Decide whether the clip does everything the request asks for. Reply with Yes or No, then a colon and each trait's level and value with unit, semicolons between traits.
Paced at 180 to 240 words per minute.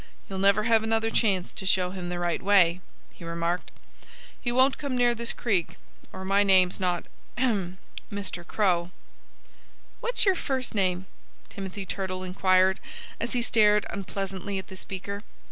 No: average, 155 wpm